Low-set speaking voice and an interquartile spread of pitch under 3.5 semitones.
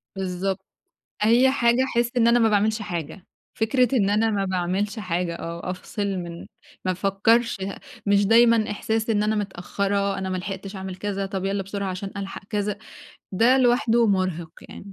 No: high, 200 Hz; average, 2.9 semitones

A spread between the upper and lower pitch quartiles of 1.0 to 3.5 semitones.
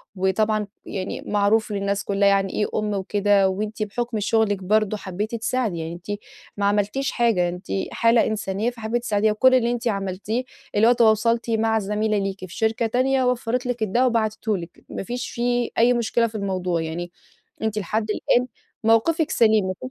Yes: average, 2.7 semitones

